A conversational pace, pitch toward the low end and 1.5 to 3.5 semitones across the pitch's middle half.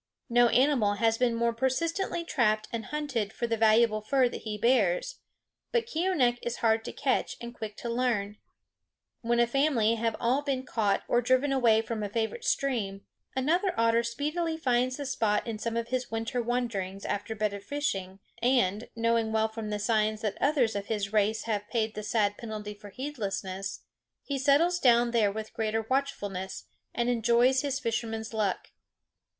No: average, 175 wpm; high, 230 Hz; average, 3.1 semitones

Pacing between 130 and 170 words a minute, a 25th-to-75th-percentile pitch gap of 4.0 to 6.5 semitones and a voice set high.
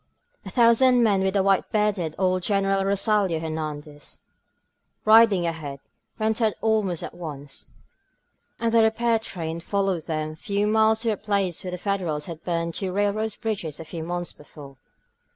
Yes: average, 160 wpm; average, 4.7 semitones; high, 195 Hz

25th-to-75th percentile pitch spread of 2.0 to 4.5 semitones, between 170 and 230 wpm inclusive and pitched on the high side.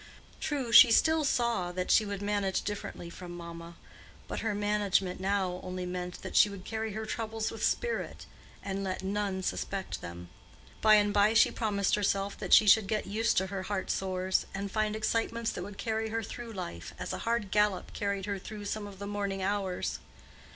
Yes: narrow, 2.4 semitones; average, 195 wpm; high, 200 Hz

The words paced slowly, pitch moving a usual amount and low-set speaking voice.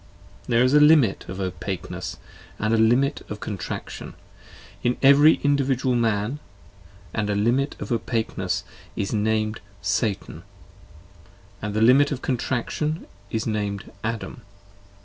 Yes: slow, 130 wpm; average, 4.3 semitones; low, 115 Hz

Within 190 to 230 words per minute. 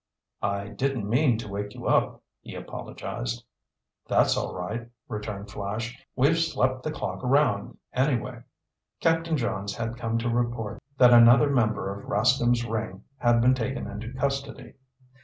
No: average, 145 wpm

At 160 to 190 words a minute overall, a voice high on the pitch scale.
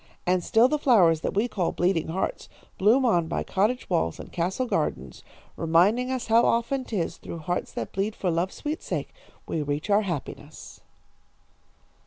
Yes: average, 170 wpm; high, 195 Hz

